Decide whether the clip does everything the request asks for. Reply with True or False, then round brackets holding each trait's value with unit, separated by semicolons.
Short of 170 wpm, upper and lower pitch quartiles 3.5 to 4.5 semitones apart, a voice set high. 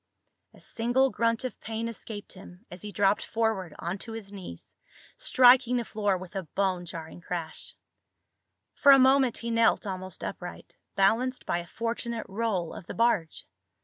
True (160 wpm; 4.0 semitones; 210 Hz)